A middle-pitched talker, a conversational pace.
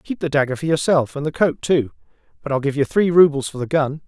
No: medium, 145 Hz; fast, 265 wpm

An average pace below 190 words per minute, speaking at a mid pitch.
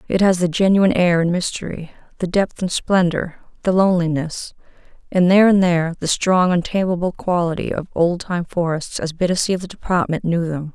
Yes: average, 180 wpm; medium, 175 Hz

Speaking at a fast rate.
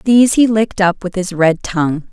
Yes: fast, 225 wpm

